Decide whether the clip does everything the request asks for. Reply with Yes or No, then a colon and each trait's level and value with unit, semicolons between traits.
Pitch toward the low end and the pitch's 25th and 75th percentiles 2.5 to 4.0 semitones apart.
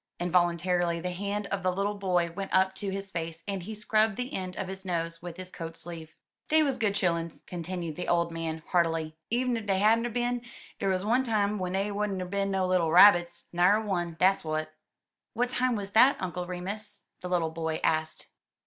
No: medium, 185 Hz; average, 3.2 semitones